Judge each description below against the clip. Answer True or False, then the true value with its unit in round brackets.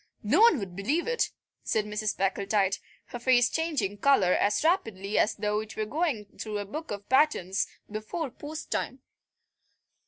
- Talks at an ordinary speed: True (160 wpm)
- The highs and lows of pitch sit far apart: True (6.6 semitones)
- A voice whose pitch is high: True (215 Hz)